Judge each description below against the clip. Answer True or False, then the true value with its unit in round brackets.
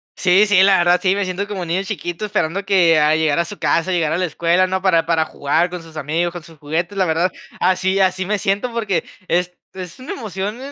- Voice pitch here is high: False (180 Hz)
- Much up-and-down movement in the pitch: False (2.7 semitones)